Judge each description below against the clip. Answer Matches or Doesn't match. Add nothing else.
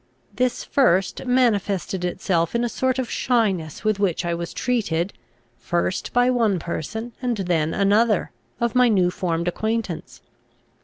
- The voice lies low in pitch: Doesn't match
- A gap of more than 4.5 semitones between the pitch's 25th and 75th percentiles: Matches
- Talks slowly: Doesn't match